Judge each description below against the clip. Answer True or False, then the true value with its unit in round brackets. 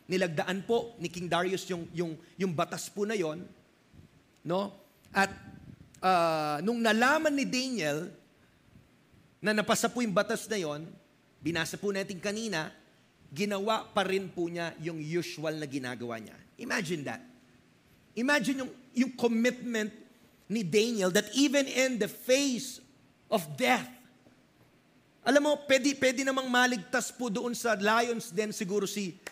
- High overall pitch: True (210 Hz)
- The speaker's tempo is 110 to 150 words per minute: True (140 wpm)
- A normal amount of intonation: False (5.7 semitones)